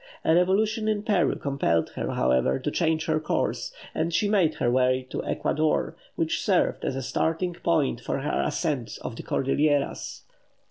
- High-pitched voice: No, medium, 155 Hz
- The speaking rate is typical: Yes, average, 170 wpm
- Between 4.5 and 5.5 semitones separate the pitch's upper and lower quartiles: Yes, average, 5.2 semitones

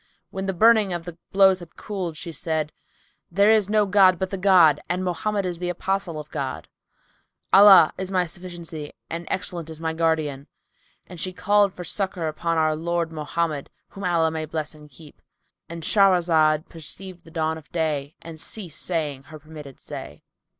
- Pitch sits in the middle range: Yes, medium, 170 Hz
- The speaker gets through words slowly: No, average, 170 wpm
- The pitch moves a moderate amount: Yes, average, 3.0 semitones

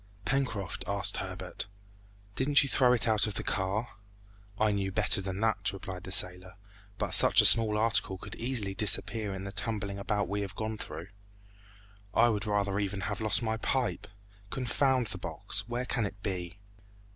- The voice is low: Yes, low, 105 Hz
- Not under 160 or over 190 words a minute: Yes, average, 175 wpm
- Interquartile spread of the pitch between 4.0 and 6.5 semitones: No, average, 2.7 semitones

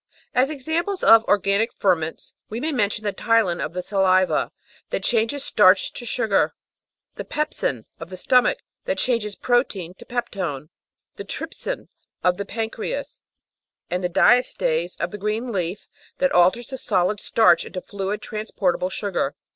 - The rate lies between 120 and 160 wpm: Yes, average, 150 wpm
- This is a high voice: Yes, high, 205 Hz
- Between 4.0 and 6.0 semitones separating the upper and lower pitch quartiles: Yes, average, 4.9 semitones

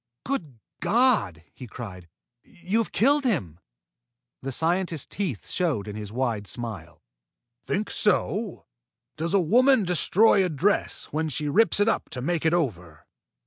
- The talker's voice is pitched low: No, medium, 160 Hz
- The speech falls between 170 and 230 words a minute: No, average, 145 wpm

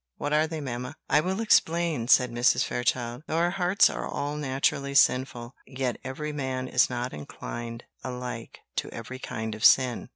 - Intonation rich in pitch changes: No, average, 3.7 semitones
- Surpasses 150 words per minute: Yes, average, 170 wpm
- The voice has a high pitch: No, low, 130 Hz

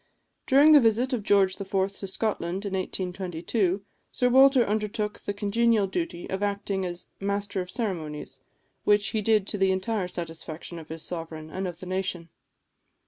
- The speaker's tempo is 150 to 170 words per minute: Yes, average, 165 wpm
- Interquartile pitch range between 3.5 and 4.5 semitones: No, average, 3.0 semitones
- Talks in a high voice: Yes, high, 195 Hz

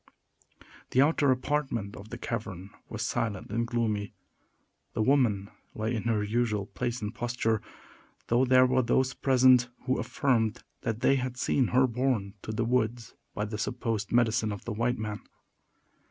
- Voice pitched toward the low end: Yes, low, 115 Hz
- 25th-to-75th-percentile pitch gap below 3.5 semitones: Yes, average, 2.9 semitones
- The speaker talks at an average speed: Yes, average, 155 wpm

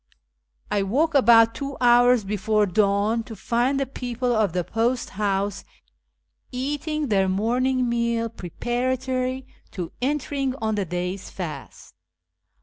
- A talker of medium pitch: No, high, 235 Hz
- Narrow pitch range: No, average, 4.2 semitones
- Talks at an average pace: No, slow, 130 wpm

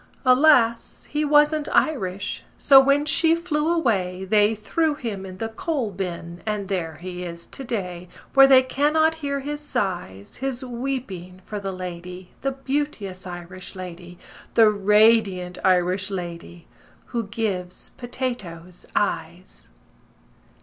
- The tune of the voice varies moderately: No, wide, 6.9 semitones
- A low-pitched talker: No, high, 210 Hz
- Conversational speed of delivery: No, slow, 130 wpm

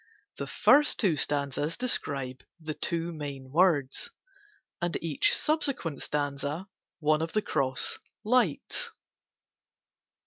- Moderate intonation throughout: Yes, average, 4.8 semitones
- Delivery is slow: Yes, slow, 105 wpm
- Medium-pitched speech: Yes, medium, 155 Hz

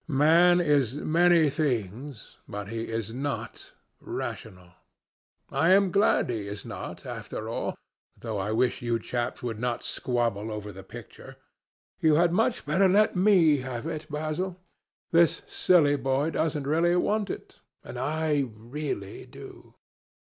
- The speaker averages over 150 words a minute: No, average, 140 wpm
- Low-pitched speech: No, medium, 145 Hz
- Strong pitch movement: Yes, wide, 6.4 semitones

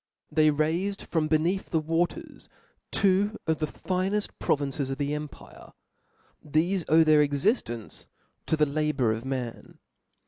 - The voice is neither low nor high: Yes, medium, 155 Hz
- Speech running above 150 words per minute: No, slow, 135 wpm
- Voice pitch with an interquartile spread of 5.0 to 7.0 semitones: No, average, 3.5 semitones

